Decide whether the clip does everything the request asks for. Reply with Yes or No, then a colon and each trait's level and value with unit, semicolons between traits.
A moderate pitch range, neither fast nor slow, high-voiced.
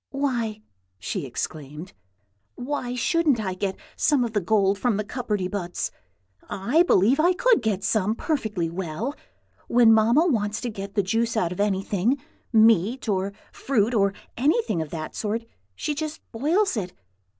Yes: average, 4.8 semitones; average, 155 wpm; high, 220 Hz